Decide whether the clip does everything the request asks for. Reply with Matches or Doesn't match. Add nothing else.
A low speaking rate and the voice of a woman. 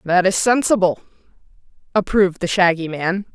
Matches